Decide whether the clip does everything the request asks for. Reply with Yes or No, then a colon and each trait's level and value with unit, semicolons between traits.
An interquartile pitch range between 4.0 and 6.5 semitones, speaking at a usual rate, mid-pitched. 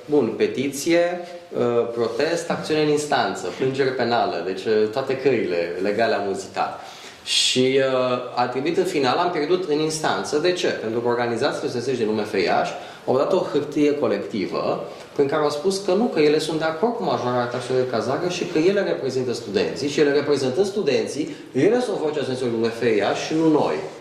No: average, 5.2 semitones; fast, 175 wpm; medium, 145 Hz